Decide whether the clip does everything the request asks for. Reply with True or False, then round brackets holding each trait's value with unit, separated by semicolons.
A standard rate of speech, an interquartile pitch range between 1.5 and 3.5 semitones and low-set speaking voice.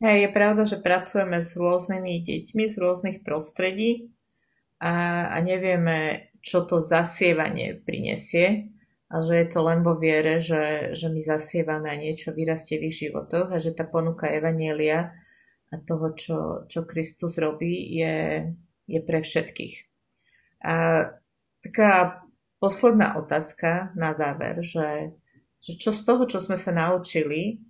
False (140 wpm; 2.6 semitones; 170 Hz)